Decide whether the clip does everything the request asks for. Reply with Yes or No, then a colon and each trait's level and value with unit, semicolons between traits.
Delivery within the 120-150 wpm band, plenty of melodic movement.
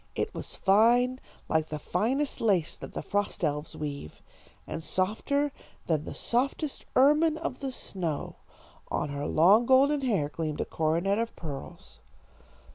Yes: average, 145 wpm; wide, 8.8 semitones